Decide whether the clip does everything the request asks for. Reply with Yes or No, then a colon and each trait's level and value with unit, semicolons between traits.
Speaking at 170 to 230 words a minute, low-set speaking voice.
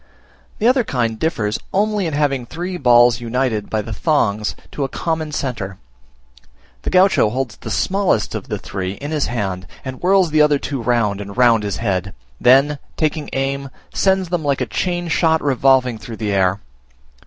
Yes: average, 175 wpm; low, 130 Hz